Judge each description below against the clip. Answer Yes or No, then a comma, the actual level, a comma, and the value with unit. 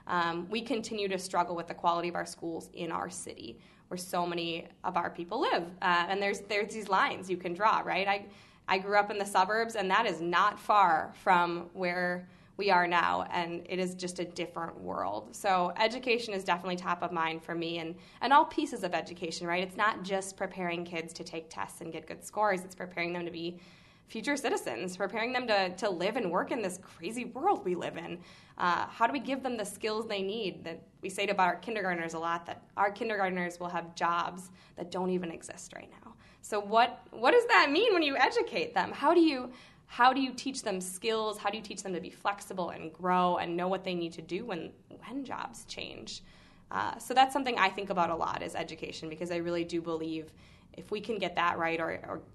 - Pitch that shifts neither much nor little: Yes, average, 4.0 semitones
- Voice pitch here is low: No, medium, 185 Hz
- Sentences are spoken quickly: Yes, fast, 230 wpm